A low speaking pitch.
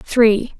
No: high, 230 Hz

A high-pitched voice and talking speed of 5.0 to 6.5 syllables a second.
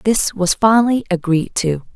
No: high, 195 Hz; 4.5 syllables/s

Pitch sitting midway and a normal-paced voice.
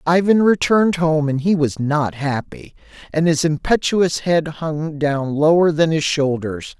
Yes: medium, 155 Hz; average, 160 wpm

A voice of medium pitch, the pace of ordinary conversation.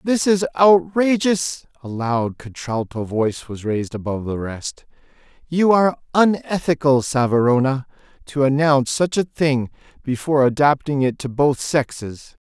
No: medium, 145 Hz; slow, 130 wpm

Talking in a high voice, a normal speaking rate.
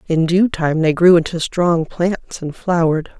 No: medium, 170 Hz; average, 190 wpm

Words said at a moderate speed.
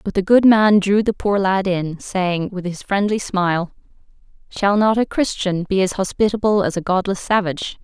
Yes: average, 190 wpm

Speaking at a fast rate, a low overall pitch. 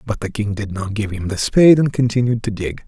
Yes: fast, 270 wpm; low, 110 Hz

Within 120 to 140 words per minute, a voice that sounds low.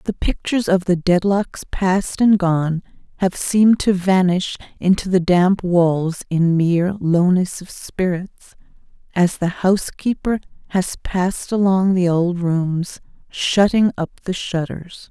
No: slow, 135 wpm; medium, 180 Hz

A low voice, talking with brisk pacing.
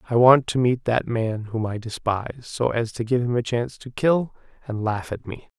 Yes: low, 120 Hz; fast, 235 wpm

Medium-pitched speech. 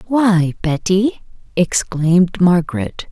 Yes: medium, 180 Hz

